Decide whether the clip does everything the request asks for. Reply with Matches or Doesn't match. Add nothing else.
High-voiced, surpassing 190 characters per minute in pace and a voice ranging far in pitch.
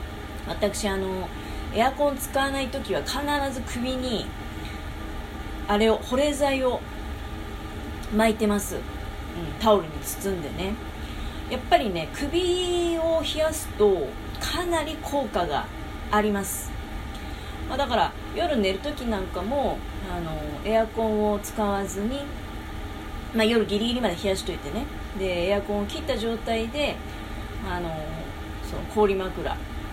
Matches